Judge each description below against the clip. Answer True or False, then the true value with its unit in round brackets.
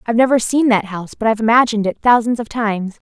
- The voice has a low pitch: False (225 Hz)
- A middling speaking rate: False (230 wpm)